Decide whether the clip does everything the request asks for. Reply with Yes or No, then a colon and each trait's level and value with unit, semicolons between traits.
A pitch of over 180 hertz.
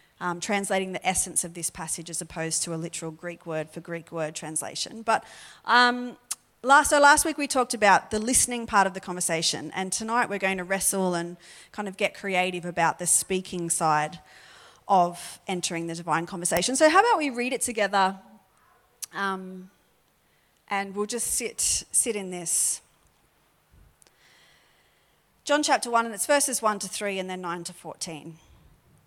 Yes: high, 190 Hz